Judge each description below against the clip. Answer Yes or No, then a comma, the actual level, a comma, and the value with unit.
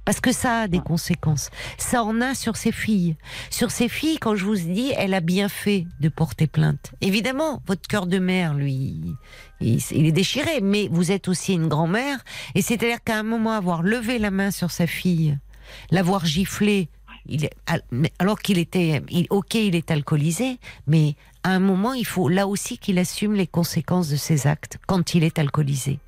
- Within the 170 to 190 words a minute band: Yes, average, 185 wpm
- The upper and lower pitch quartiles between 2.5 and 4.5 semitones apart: No, average, 4.9 semitones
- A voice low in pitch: No, medium, 185 Hz